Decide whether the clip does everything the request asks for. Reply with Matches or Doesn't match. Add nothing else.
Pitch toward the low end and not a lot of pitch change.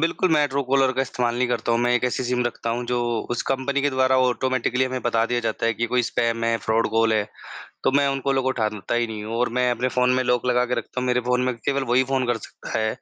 Matches